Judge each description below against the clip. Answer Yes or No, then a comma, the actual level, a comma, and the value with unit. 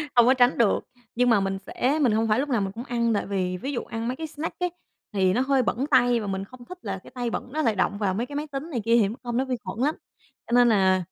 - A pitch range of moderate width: Yes, average, 4.3 semitones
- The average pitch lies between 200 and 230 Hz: No, high, 240 Hz